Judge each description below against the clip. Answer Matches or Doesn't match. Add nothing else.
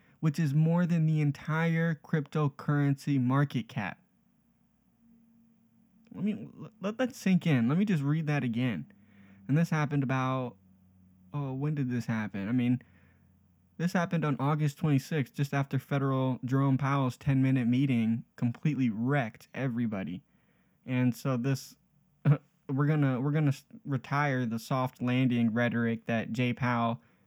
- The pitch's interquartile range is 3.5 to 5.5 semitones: Matches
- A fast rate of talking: Doesn't match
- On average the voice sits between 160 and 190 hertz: Doesn't match